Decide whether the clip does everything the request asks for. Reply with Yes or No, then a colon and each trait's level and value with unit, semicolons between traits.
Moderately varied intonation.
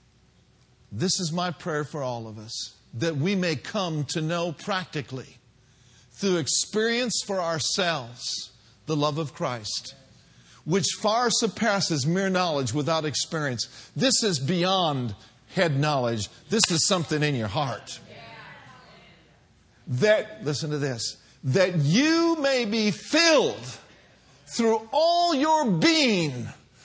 No: wide, 7.2 semitones